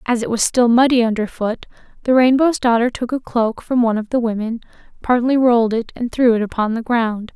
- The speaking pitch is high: Yes, high, 235 Hz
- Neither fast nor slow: No, fast, 210 wpm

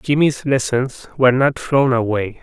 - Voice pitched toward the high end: No, low, 130 Hz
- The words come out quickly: No, average, 150 wpm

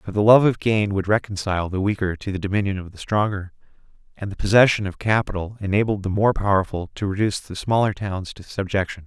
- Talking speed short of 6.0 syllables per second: No, 6.1 syllables/s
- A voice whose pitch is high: No, low, 100 Hz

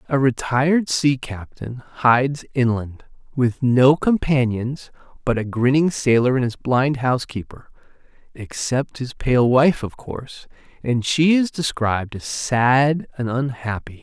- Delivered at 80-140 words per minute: Yes, slow, 135 wpm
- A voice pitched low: Yes, low, 130 Hz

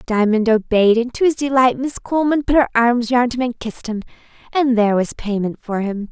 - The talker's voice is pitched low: No, high, 240 Hz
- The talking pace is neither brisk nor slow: No, fast, 215 wpm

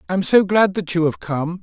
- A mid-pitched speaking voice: Yes, medium, 175 Hz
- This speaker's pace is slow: No, fast, 295 wpm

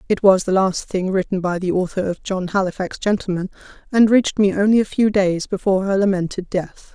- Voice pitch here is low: No, high, 190 Hz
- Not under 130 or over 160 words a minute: No, fast, 205 wpm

